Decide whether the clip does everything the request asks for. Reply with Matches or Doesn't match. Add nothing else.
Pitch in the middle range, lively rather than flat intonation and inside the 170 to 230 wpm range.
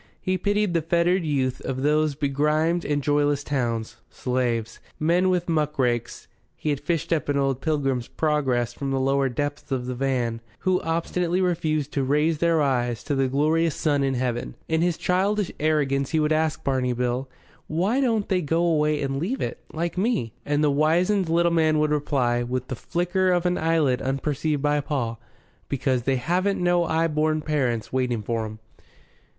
Doesn't match